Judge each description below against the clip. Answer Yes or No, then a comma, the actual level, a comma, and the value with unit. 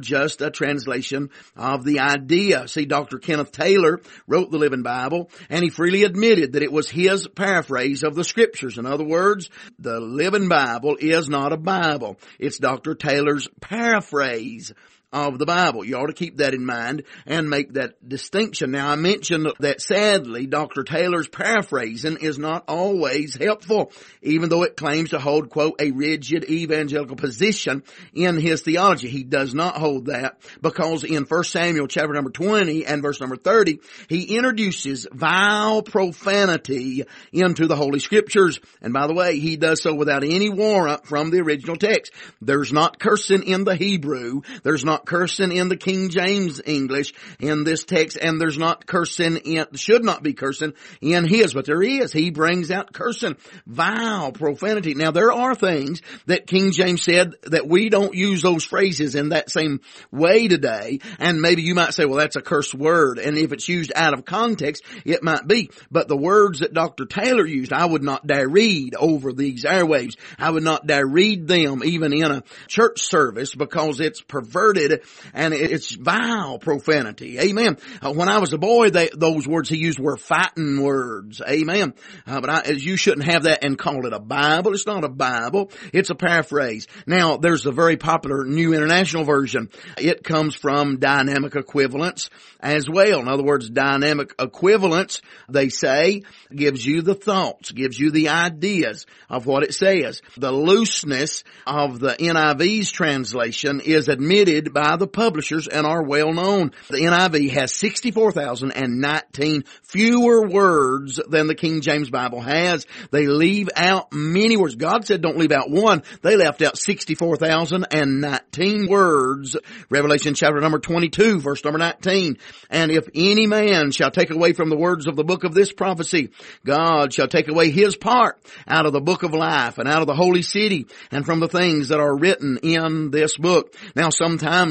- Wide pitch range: No, average, 4.2 semitones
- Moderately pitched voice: Yes, medium, 160 Hz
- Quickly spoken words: No, average, 175 wpm